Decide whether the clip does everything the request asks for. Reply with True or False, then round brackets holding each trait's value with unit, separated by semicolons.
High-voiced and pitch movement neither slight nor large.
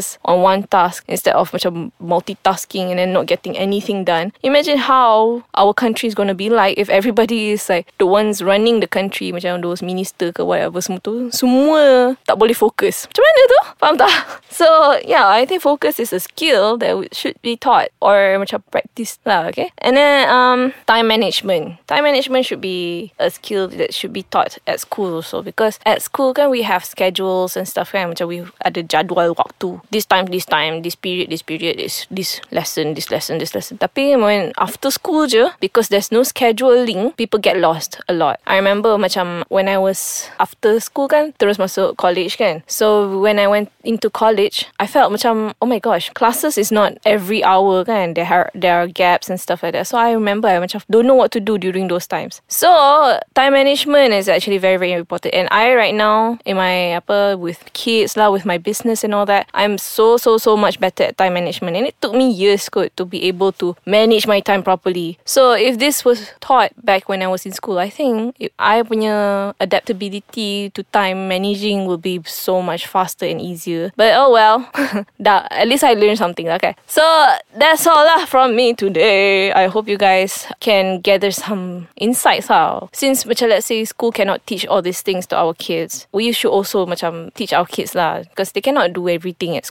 True (205 Hz; 4.2 semitones)